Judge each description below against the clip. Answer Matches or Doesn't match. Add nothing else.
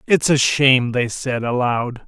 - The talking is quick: Doesn't match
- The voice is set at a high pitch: Doesn't match